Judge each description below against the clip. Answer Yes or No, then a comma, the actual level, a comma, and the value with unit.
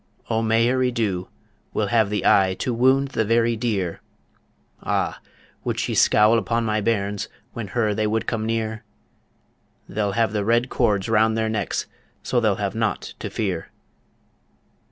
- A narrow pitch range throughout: Yes, narrow, 2.0 semitones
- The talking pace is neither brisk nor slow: Yes, average, 155 wpm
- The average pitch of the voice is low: Yes, low, 110 Hz